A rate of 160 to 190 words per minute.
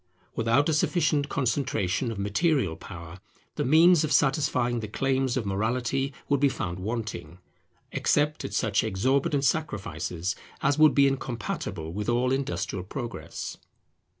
No: slow, 135 wpm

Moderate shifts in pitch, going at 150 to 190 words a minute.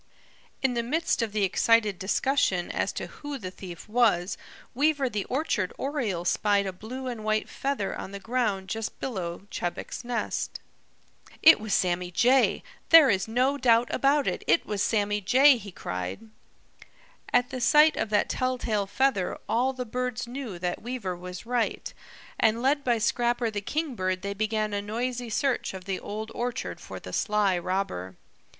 Yes: average, 4.4 semitones; average, 170 wpm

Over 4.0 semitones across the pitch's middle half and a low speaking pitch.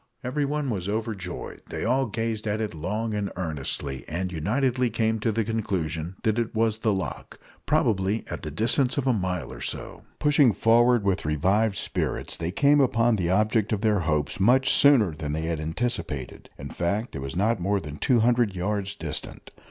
Yes: average, 5.1 semitones; low, 105 Hz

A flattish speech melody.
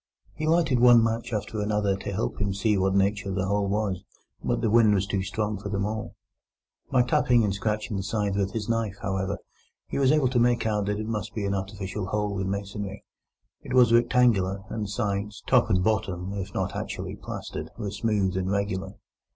Yes: narrow, 2.3 semitones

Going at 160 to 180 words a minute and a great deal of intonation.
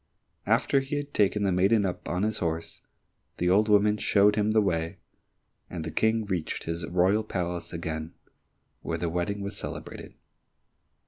No: average, 165 wpm; average, 3.5 semitones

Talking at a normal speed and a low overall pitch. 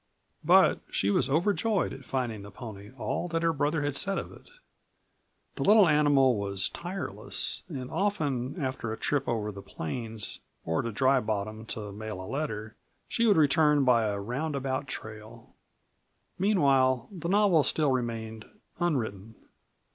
Yes: average, 150 wpm; low, 130 Hz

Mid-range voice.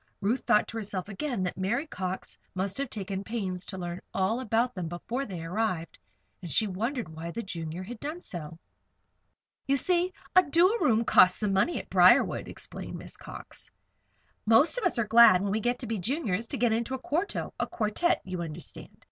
No: high, 215 Hz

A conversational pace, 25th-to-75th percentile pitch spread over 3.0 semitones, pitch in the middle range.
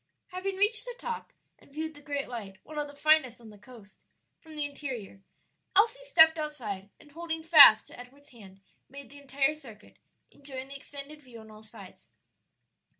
No: average, 180 wpm; average, 4.9 semitones; very high, 285 Hz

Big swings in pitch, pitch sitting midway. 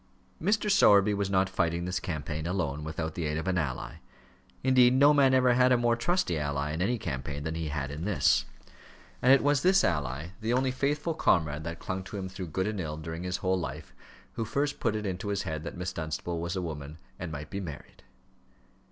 No: wide, 7.0 semitones; very low, 90 Hz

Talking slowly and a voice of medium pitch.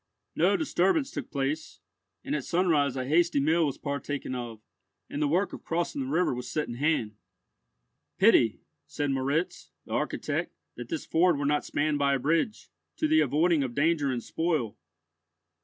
No: average, 175 wpm; medium, 150 Hz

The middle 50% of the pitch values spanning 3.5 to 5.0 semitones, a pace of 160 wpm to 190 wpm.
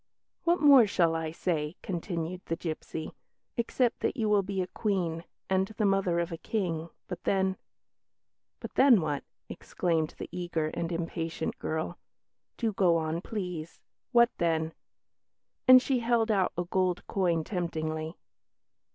No: average, 3.8 semitones; average, 150 wpm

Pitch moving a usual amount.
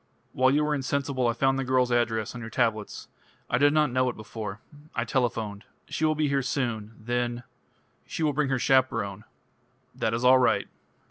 Yes: average, 3.1 semitones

